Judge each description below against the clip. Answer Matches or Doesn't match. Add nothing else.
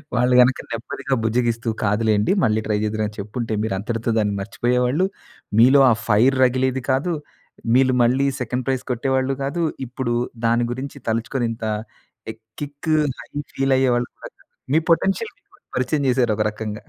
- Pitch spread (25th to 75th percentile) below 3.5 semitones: Matches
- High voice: Doesn't match